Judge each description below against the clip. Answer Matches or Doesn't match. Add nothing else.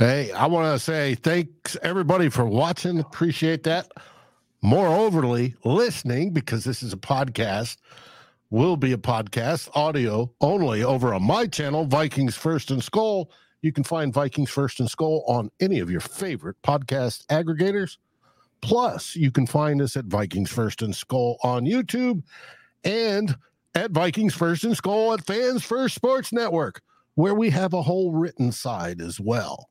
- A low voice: Doesn't match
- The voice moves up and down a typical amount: Doesn't match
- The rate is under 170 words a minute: Matches